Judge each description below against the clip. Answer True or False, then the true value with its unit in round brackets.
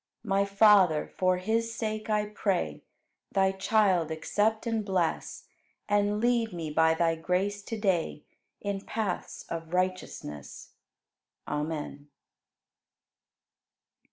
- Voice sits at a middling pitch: False (195 Hz)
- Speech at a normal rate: False (105 wpm)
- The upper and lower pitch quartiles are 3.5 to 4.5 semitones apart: True (4.2 semitones)